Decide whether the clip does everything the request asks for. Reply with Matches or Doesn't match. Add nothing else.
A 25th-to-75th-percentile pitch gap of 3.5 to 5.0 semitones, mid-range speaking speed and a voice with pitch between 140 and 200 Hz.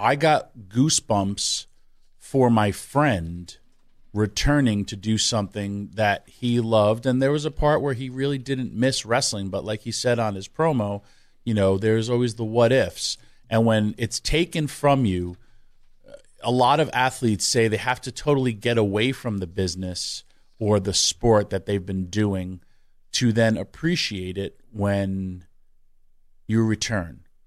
Doesn't match